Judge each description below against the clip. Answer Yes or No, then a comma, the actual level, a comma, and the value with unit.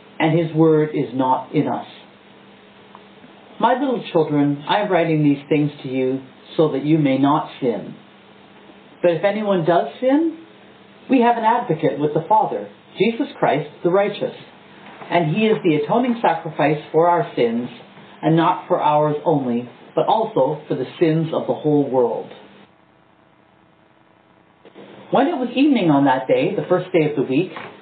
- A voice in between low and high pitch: Yes, medium, 165 Hz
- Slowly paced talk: No, average, 160 wpm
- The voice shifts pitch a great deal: Yes, wide, 5.8 semitones